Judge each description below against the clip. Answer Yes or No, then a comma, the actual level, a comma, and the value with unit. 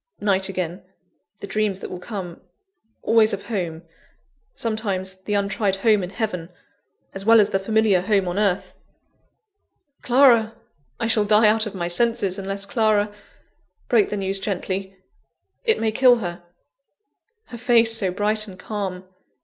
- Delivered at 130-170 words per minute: Yes, average, 150 wpm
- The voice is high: Yes, high, 205 Hz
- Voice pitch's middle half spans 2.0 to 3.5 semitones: Yes, narrow, 2.6 semitones